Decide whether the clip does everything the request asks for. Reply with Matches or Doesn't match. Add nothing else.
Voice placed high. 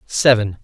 Doesn't match